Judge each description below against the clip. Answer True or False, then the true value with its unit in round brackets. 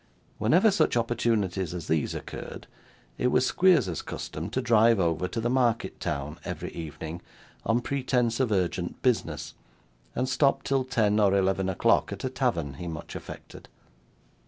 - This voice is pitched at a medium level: False (105 Hz)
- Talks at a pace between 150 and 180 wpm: True (155 wpm)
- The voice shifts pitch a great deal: True (6.2 semitones)